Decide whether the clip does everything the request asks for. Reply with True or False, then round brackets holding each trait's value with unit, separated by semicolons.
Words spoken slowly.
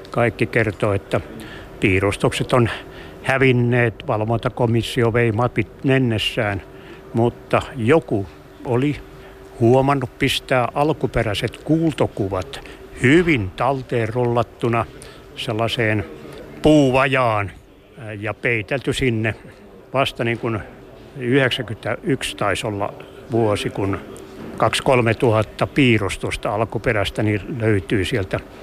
True (80 wpm)